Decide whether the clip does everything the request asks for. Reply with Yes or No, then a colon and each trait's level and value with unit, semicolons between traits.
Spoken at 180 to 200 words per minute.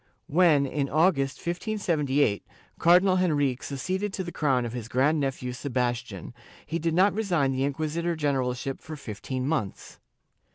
No: average, 150 wpm